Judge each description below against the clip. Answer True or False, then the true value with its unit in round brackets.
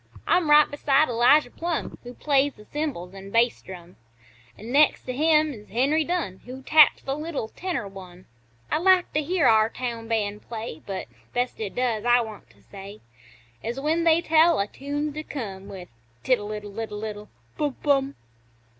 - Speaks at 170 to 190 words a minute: True (180 wpm)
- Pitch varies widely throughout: True (6.2 semitones)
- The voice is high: True (250 Hz)